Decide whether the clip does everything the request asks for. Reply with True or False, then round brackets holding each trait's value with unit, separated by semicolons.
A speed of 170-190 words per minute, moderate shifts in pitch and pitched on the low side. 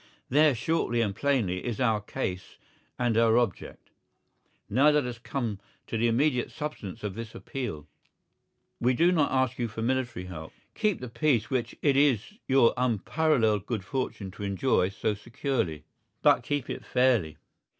False (160 wpm; 4.3 semitones; 120 Hz)